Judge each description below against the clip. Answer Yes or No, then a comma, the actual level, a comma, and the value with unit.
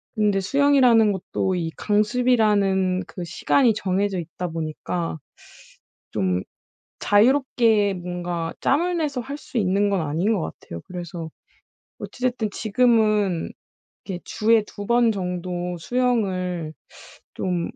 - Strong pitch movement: No, average, 4.5 semitones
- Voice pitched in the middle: No, high, 200 Hz